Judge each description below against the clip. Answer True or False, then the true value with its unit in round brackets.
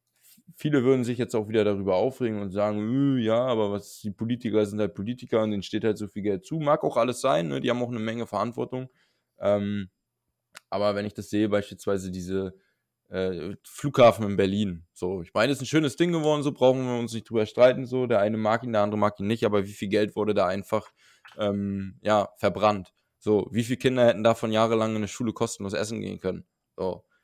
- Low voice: True (110 Hz)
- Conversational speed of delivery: False (220 wpm)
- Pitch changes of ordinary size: True (3.1 semitones)